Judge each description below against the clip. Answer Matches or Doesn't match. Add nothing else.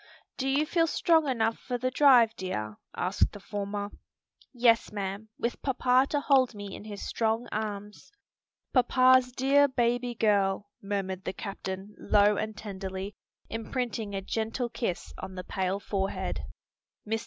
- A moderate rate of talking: Matches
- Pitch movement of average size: Matches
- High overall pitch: Matches